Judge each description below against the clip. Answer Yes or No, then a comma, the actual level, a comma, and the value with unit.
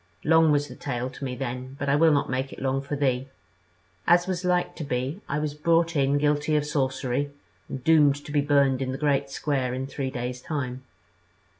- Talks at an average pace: No, fast, 210 wpm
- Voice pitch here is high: No, medium, 140 Hz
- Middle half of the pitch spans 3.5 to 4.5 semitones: No, narrow, 2.4 semitones